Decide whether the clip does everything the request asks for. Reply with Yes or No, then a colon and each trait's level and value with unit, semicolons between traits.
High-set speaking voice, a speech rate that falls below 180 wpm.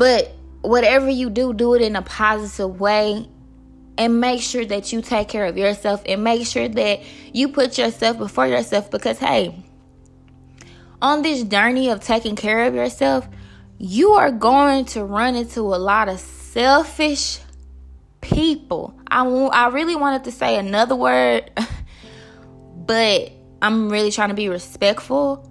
Yes: high, 220 Hz; average, 155 wpm